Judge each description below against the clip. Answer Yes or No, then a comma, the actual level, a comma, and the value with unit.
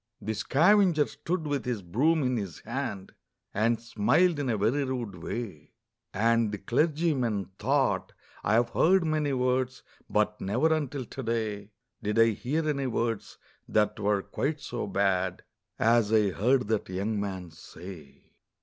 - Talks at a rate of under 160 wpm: Yes, average, 150 wpm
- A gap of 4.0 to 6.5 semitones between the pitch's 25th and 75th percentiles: Yes, average, 5.3 semitones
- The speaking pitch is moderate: No, low, 115 Hz